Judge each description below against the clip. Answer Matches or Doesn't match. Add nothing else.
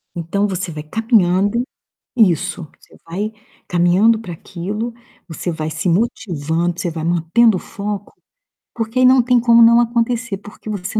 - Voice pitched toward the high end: Matches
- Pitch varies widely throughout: Doesn't match